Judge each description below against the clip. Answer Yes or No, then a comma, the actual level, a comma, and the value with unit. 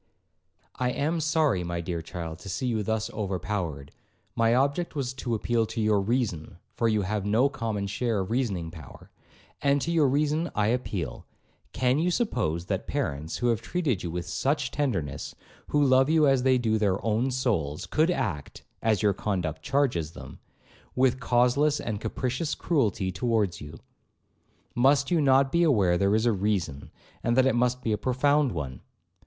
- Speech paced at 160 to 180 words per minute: Yes, average, 170 wpm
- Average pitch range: No, wide, 6.0 semitones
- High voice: No, low, 115 Hz